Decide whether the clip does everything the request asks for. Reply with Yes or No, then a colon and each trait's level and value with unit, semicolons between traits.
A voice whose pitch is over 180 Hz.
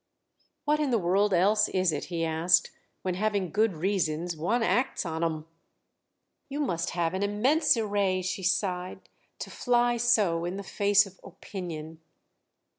Yes: high, 190 Hz